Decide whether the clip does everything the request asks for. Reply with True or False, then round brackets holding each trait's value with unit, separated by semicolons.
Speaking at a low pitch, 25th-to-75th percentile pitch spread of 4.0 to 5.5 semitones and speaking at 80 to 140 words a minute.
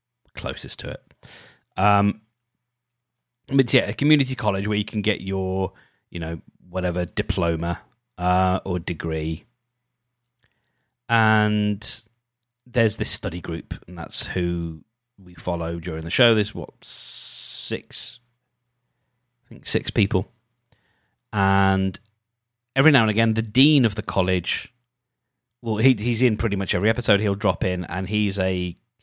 True (105 Hz; 4.6 semitones; 135 wpm)